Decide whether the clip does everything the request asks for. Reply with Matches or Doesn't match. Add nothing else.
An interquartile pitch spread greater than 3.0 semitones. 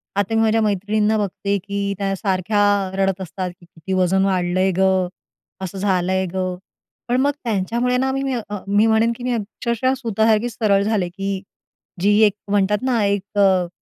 Doesn't match